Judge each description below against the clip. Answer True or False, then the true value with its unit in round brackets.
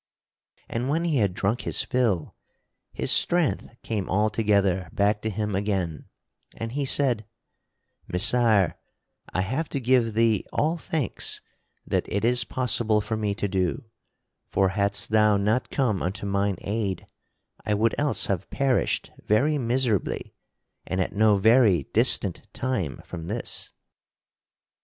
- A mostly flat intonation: False (3.7 semitones)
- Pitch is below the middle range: True (110 Hz)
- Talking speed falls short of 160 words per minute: True (140 wpm)